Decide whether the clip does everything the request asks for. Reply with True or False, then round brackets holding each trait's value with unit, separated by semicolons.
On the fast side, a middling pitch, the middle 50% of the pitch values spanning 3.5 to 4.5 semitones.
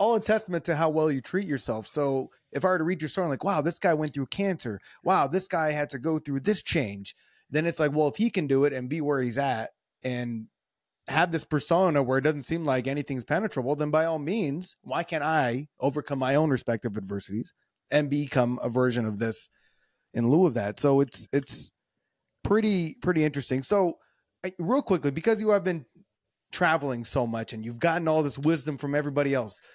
True (215 wpm; 150 Hz; 4.2 semitones)